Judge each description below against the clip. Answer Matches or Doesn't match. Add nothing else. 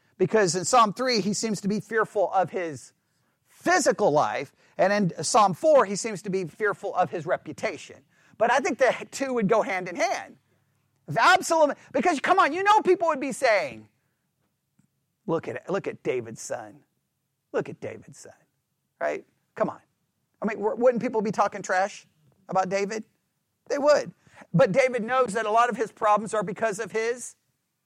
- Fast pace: Doesn't match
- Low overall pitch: Doesn't match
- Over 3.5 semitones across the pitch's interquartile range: Matches